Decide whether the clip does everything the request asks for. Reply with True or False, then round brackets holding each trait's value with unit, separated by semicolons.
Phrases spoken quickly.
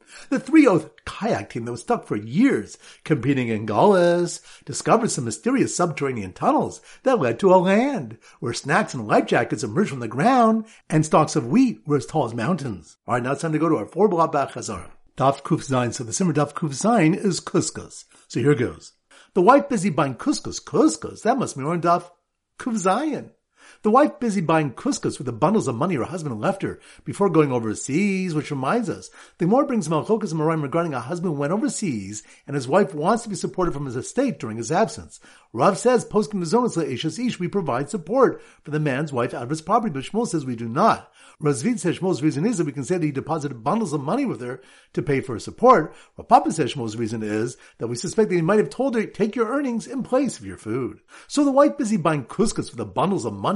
True (220 wpm)